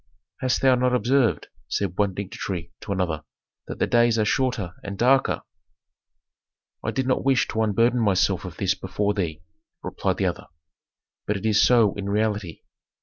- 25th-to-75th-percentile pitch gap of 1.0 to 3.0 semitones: No, average, 4.3 semitones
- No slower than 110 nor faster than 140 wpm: No, average, 165 wpm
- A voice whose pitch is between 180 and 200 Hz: No, low, 105 Hz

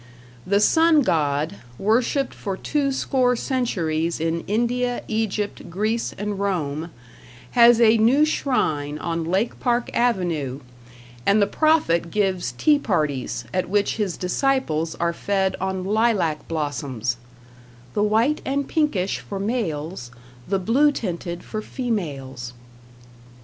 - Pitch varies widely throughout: Yes, wide, 6.5 semitones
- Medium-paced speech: No, slow, 125 wpm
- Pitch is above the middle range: Yes, high, 200 Hz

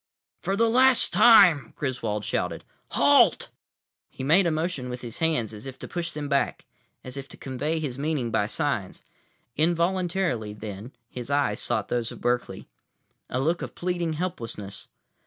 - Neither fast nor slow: Yes, average, 160 wpm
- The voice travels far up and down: Yes, wide, 5.9 semitones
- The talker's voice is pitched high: No, medium, 140 Hz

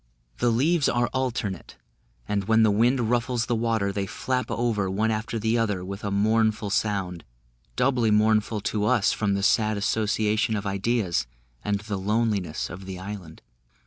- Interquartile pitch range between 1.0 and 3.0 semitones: Yes, narrow, 2.5 semitones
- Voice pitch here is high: No, low, 110 Hz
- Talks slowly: No, average, 165 wpm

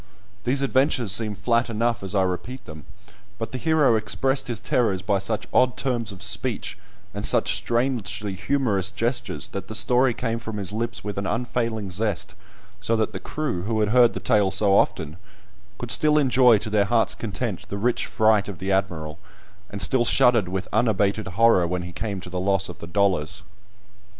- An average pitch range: Yes, average, 3.7 semitones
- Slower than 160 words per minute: No, average, 190 wpm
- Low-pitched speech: Yes, low, 110 Hz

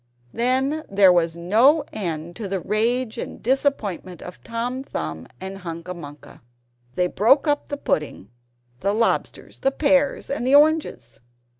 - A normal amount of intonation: No, wide, 7.6 semitones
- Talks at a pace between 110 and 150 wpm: Yes, average, 145 wpm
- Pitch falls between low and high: No, high, 215 Hz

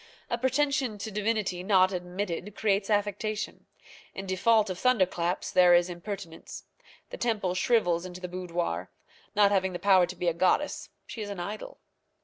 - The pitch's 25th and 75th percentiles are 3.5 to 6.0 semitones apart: No, average, 3.1 semitones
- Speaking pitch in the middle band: No, high, 195 Hz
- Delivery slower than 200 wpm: Yes, average, 160 wpm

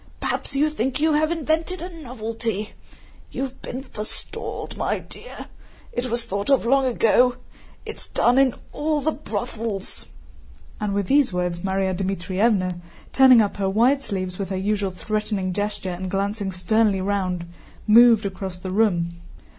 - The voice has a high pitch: Yes, high, 215 Hz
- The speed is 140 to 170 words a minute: Yes, average, 155 wpm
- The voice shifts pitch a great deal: No, average, 4.9 semitones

